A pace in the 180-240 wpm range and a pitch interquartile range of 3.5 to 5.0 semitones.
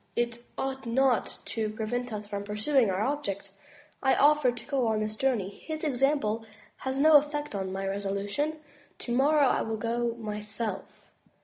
No: average, 165 wpm; average, 4.4 semitones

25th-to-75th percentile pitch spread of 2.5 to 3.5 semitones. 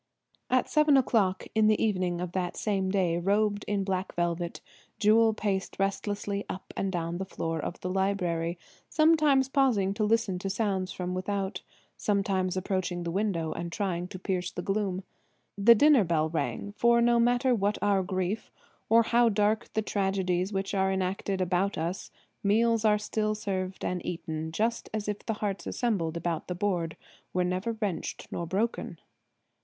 Yes: average, 2.9 semitones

